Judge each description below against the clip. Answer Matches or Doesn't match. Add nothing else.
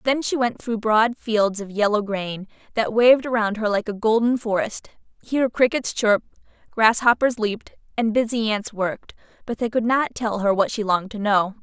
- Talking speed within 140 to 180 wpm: Doesn't match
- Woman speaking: Matches